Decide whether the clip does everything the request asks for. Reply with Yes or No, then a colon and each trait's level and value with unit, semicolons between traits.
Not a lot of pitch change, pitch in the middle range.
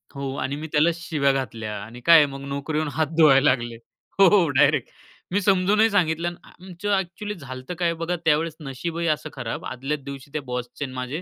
No: average, 4.2 semitones; medium, 150 Hz